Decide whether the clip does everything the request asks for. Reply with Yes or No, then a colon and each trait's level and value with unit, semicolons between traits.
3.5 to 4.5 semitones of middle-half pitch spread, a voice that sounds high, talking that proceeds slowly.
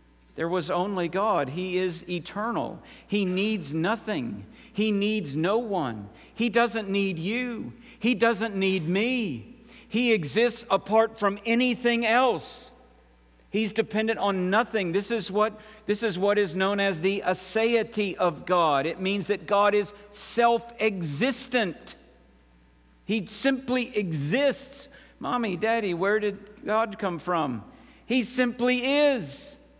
Yes: average, 4.0 semitones; high, 210 Hz; slow, 130 wpm